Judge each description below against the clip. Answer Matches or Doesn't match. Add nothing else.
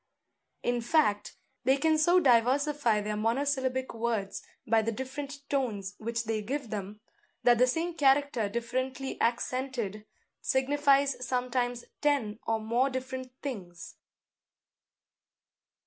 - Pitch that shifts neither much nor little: Matches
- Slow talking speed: Matches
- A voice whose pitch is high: Matches